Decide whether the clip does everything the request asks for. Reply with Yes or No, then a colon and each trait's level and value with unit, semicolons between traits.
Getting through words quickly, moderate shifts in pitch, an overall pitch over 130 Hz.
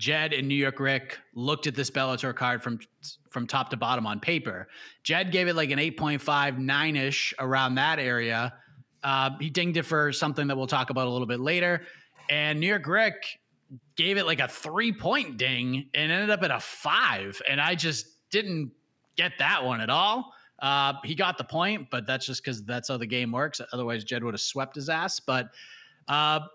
Yes: fast, 210 wpm; average, 3.8 semitones; medium, 140 Hz